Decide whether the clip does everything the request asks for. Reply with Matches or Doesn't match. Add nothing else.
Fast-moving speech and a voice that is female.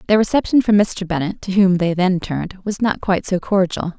Matches